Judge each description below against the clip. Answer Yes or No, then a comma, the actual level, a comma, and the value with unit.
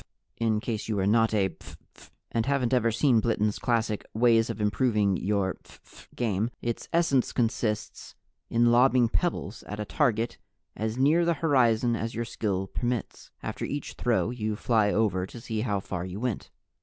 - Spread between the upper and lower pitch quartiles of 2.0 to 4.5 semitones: Yes, narrow, 2.5 semitones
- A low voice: Yes, low, 115 Hz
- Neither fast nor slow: Yes, average, 175 wpm